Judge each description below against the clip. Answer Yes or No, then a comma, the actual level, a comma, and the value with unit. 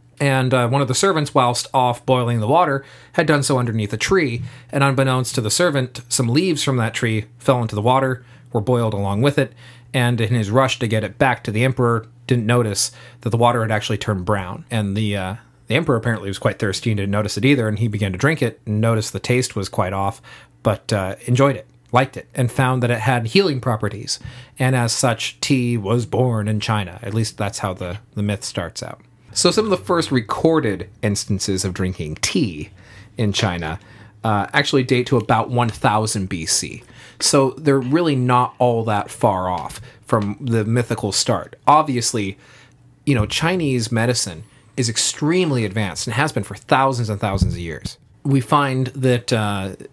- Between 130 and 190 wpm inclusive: No, average, 200 wpm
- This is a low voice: Yes, low, 120 Hz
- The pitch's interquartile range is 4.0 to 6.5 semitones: No, average, 3.6 semitones